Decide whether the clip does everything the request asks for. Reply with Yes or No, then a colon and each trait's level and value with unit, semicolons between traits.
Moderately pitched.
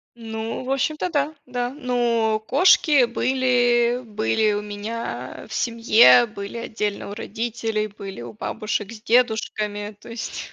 No: high, 230 Hz